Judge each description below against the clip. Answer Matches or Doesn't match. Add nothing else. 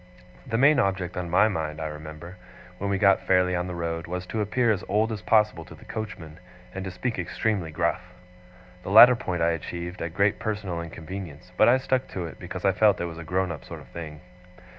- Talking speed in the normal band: Doesn't match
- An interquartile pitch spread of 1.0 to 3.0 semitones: Doesn't match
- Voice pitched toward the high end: Doesn't match